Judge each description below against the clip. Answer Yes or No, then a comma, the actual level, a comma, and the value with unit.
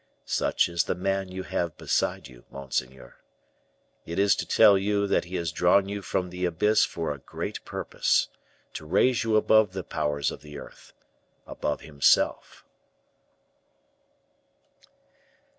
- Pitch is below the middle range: Yes, very low, 90 Hz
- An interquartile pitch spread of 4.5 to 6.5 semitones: Yes, average, 4.9 semitones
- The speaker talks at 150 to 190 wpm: No, average, 140 wpm